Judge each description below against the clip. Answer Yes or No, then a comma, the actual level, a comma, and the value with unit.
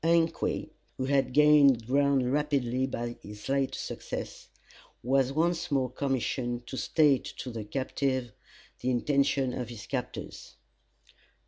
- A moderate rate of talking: No, slow, 125 wpm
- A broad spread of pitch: No, narrow, 2.4 semitones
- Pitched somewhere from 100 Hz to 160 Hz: Yes, low, 135 Hz